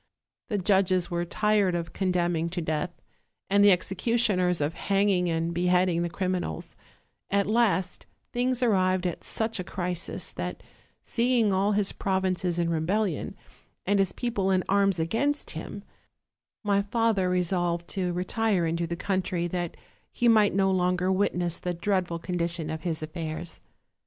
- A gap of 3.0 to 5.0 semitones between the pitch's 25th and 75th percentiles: No, narrow, 2.6 semitones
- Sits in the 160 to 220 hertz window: Yes, medium, 185 Hz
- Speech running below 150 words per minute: No, average, 155 wpm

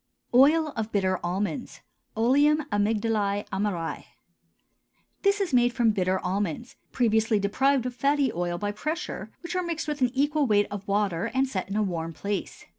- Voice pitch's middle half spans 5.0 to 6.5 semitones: Yes, wide, 5.6 semitones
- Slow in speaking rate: No, average, 165 wpm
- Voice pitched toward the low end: No, high, 220 Hz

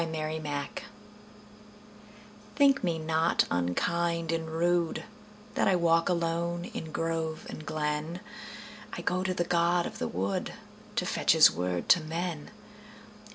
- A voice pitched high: No, medium, 165 Hz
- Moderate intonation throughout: No, narrow, 1.8 semitones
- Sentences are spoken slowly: Yes, slow, 120 wpm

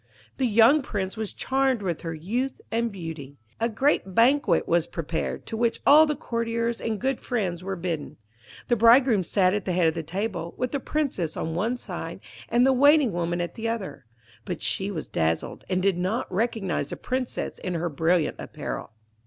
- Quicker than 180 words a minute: Yes, average, 190 wpm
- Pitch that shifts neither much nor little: No, wide, 5.7 semitones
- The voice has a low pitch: No, high, 205 Hz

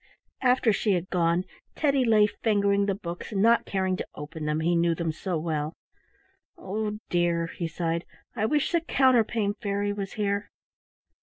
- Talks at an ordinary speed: Yes, average, 165 wpm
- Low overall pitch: No, high, 200 Hz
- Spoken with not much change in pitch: No, average, 4.3 semitones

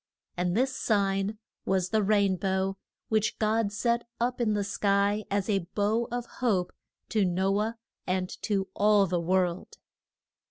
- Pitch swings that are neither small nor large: No, narrow, 2.3 semitones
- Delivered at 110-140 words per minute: No, average, 155 wpm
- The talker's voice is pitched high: Yes, high, 200 Hz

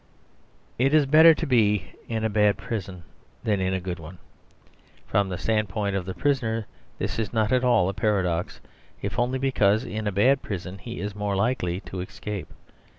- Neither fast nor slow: Yes, average, 185 wpm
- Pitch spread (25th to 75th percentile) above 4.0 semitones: No, average, 3.7 semitones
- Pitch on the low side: Yes, low, 105 Hz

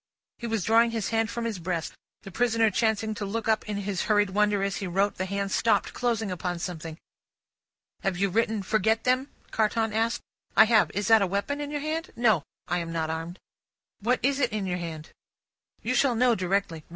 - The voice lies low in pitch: No, high, 210 Hz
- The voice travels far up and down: No, average, 3.5 semitones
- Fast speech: Yes, fast, 210 wpm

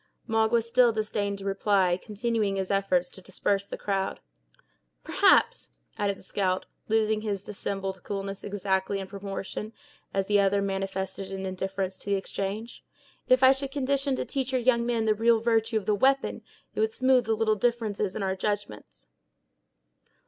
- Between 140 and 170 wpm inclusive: Yes, average, 165 wpm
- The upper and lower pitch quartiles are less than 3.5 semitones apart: Yes, average, 2.7 semitones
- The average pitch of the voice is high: Yes, high, 205 Hz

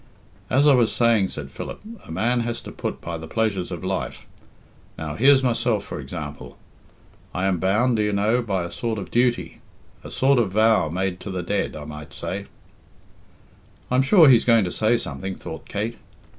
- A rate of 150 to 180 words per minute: No, average, 195 wpm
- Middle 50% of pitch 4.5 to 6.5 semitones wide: Yes, average, 4.8 semitones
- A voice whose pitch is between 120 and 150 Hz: No, low, 105 Hz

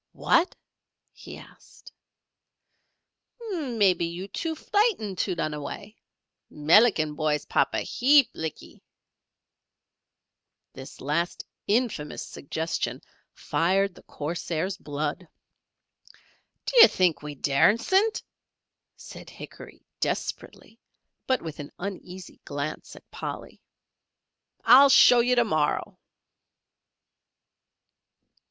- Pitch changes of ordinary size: No, wide, 7.8 semitones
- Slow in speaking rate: Yes, slow, 90 wpm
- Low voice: No, medium, 185 Hz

